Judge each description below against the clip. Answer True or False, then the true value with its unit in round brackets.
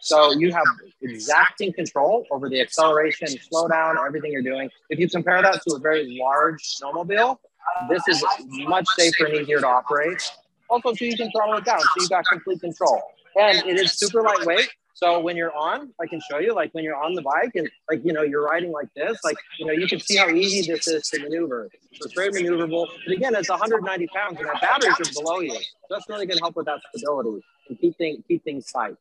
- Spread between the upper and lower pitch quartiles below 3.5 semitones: False (4.0 semitones)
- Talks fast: True (225 wpm)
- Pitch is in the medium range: True (170 Hz)